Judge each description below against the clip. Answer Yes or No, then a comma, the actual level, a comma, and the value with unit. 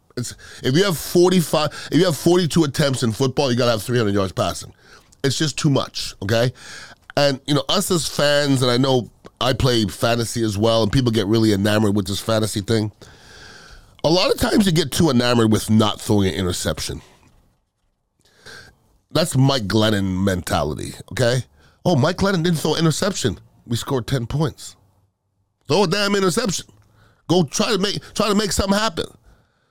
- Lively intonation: Yes, wide, 6.7 semitones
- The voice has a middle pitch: No, low, 125 Hz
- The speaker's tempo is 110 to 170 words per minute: No, average, 180 wpm